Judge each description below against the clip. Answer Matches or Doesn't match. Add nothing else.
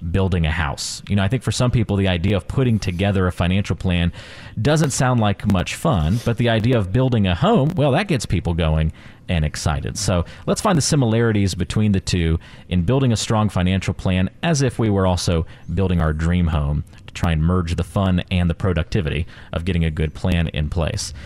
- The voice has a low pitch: Matches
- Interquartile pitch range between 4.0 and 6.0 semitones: Matches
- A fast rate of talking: Matches